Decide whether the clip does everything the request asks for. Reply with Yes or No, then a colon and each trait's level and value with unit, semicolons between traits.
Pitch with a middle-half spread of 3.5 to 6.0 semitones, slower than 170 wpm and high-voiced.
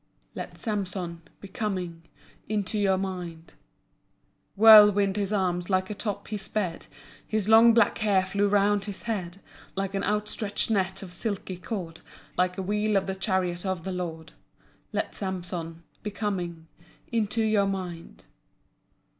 No: narrow, 2.4 semitones; average, 145 wpm; high, 195 Hz